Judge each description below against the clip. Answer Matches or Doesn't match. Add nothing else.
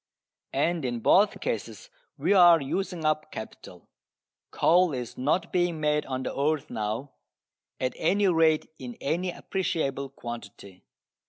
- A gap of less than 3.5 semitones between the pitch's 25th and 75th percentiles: Doesn't match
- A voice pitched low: Doesn't match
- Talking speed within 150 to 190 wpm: Doesn't match